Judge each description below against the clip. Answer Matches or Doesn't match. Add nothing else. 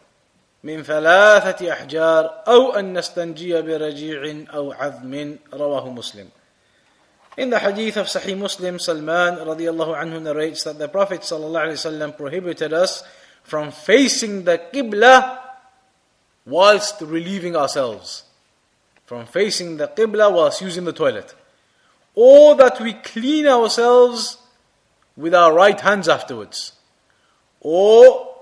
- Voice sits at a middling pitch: Matches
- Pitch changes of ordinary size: Doesn't match